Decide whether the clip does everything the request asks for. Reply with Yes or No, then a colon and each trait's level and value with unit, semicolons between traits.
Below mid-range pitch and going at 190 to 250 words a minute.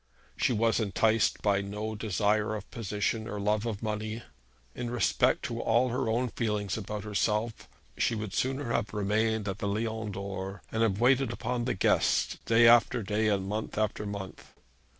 No: low, 110 Hz; average, 170 wpm